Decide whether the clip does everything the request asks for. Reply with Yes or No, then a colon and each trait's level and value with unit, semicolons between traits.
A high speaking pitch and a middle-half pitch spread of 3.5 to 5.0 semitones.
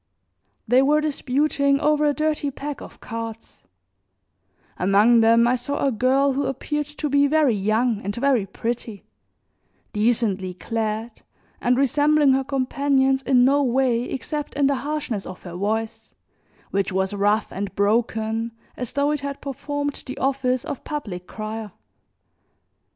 Yes: very high, 255 Hz; average, 4.3 semitones